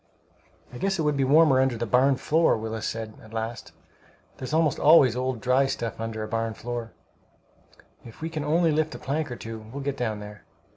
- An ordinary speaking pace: No, fast, 210 wpm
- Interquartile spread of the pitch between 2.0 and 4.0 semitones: No, average, 4.8 semitones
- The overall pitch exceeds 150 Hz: No, low, 125 Hz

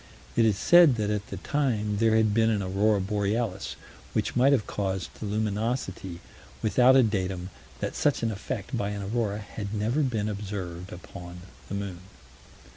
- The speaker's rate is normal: Yes, average, 170 wpm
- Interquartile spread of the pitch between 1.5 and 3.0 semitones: Yes, narrow, 2.6 semitones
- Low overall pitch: Yes, low, 105 Hz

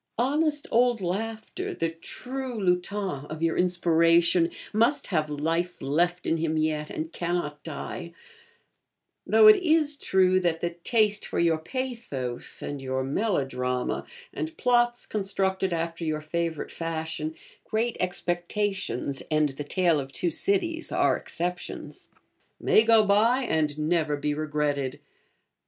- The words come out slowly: Yes, slow, 130 wpm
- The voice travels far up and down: Yes, wide, 6.0 semitones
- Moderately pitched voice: Yes, medium, 175 Hz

